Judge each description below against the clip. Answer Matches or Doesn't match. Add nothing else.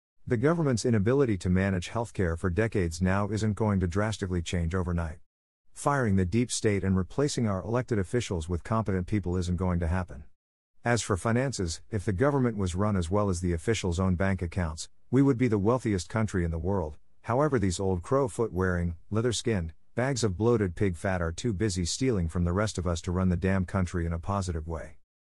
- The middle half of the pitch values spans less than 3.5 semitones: Doesn't match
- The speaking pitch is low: Matches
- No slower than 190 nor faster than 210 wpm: Matches